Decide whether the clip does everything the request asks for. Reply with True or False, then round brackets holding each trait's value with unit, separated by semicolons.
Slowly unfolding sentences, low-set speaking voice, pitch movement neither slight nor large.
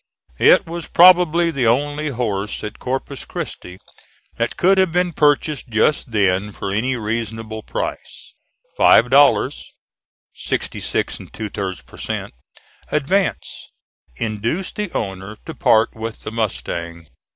False (130 wpm; 115 Hz; 6.3 semitones)